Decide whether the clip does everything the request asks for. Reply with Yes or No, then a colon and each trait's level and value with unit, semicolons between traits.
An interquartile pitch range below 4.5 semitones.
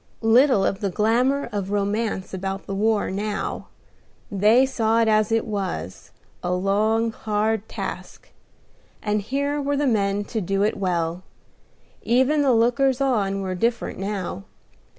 Yes: average, 3.2 semitones